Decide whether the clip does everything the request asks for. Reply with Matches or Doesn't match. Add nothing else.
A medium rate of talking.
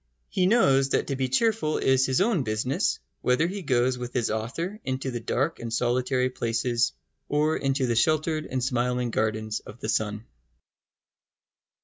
Matches